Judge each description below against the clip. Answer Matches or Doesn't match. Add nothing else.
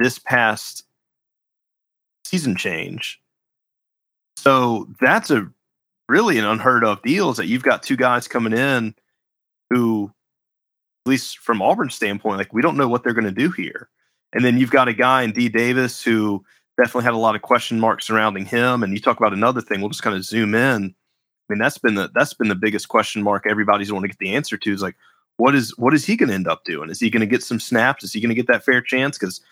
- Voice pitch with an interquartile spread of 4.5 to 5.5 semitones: Doesn't match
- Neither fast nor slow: Doesn't match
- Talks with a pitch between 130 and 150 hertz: Doesn't match